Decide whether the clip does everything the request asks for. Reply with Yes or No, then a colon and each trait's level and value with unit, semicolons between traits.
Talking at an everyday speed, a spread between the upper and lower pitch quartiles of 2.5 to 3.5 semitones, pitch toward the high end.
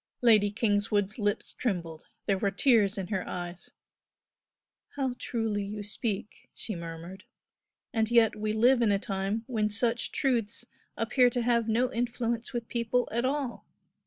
Yes: average, 150 wpm; average, 2.9 semitones; high, 220 Hz